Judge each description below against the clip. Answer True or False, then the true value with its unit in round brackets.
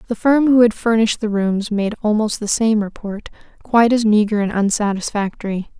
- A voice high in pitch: True (215 Hz)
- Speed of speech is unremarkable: True (175 wpm)